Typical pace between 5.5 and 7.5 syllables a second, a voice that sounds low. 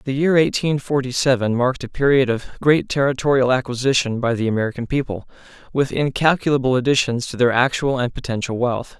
Yes: 5.9 syllables/s; low, 130 Hz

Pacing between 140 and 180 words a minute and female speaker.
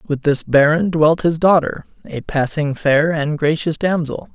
No: average, 165 wpm; male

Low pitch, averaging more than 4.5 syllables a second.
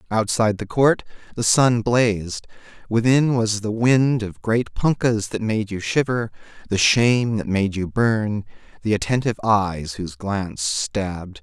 No: low, 110 Hz; 4.4 syllables/s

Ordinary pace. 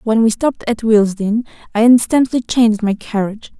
Yes: average, 165 wpm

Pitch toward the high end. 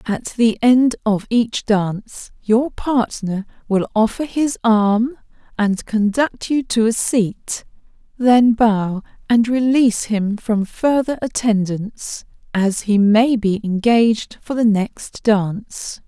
Yes: high, 225 Hz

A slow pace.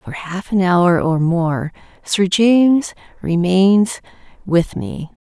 Yes: slow, 125 wpm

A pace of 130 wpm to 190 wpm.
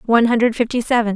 No: fast, 205 wpm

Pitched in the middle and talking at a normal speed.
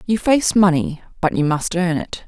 No: medium, 180 Hz; fast, 210 wpm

